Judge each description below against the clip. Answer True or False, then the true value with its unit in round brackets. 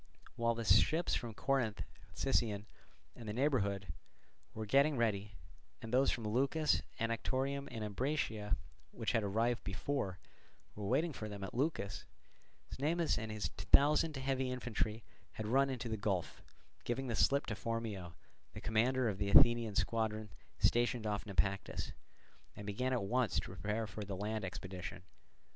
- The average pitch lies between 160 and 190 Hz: False (115 Hz)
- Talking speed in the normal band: True (150 wpm)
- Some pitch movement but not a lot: True (3.9 semitones)